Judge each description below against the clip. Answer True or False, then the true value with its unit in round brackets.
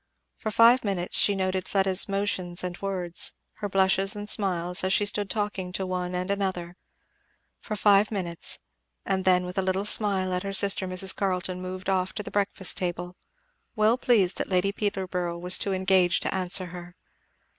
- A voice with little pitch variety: True (1.7 semitones)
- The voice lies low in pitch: False (190 Hz)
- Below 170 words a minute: False (175 wpm)